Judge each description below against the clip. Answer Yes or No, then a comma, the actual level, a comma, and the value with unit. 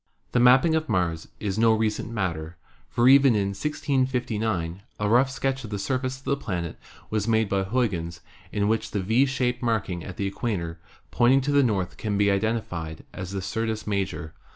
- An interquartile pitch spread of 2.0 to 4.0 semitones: No, average, 4.6 semitones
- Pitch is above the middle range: No, low, 110 Hz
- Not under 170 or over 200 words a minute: Yes, average, 185 wpm